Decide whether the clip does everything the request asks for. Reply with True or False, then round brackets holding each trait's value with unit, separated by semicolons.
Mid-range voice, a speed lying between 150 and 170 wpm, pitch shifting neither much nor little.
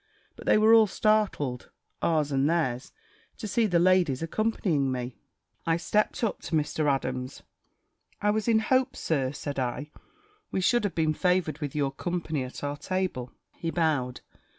False (160 Hz; 165 wpm; 6.1 semitones)